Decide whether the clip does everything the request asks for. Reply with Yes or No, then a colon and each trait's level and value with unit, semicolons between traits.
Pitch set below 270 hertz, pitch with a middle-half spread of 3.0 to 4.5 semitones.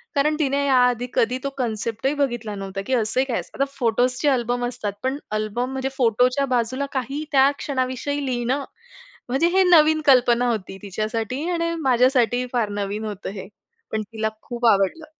Yes: very high, 250 Hz; average, 3.6 semitones